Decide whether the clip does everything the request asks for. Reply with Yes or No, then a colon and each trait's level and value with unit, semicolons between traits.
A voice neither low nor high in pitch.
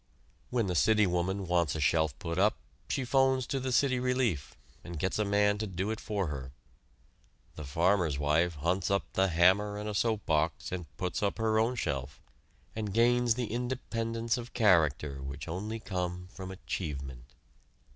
No: very low, 95 Hz